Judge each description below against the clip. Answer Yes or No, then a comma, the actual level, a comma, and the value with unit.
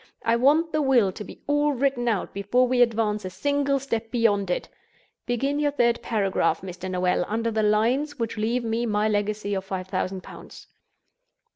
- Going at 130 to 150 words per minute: No, average, 180 wpm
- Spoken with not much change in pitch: No, average, 4.1 semitones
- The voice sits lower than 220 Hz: No, high, 230 Hz